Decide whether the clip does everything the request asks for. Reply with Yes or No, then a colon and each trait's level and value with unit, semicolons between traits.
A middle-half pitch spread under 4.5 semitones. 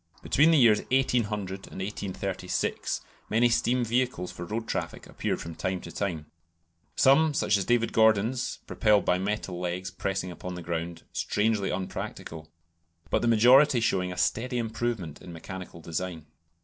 No: average, 4.8 semitones